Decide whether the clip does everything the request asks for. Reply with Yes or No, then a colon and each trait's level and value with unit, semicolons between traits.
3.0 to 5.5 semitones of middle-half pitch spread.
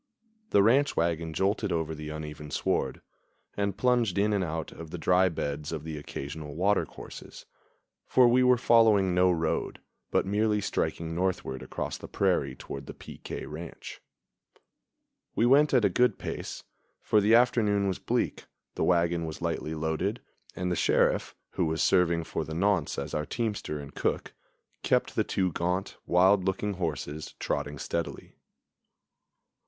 Yes: average, 4.5 semitones